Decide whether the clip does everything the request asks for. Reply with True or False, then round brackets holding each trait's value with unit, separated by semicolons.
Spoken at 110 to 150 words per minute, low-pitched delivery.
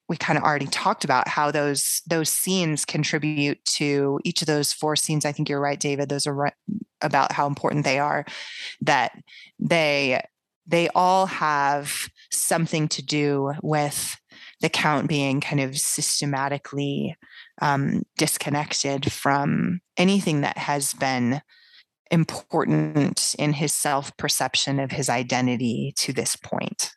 False (140 wpm; 145 Hz)